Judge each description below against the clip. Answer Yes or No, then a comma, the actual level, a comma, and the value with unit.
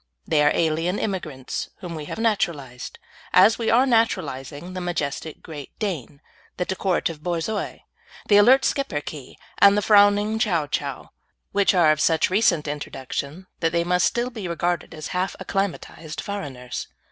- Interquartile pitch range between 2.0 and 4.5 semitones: No, average, 5.2 semitones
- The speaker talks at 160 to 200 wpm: No, average, 150 wpm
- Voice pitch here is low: No, medium, 175 Hz